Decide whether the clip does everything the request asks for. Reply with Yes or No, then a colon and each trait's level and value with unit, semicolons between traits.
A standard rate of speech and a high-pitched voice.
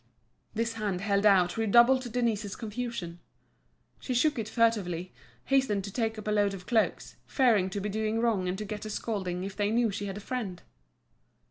Yes: average, 190 wpm; high, 210 Hz